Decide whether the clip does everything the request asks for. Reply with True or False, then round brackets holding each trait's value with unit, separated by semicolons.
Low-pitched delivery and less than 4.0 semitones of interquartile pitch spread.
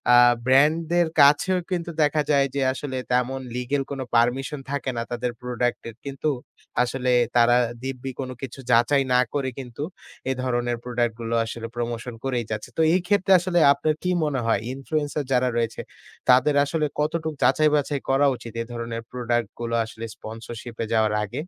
True (130 Hz; 3.4 semitones)